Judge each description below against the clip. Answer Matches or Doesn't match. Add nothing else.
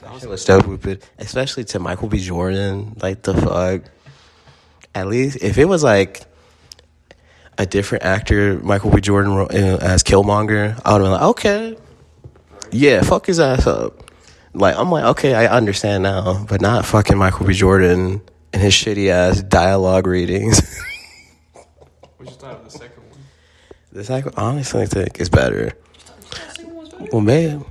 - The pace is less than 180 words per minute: Matches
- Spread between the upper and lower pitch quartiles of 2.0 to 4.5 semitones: Matches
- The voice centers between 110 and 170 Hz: Doesn't match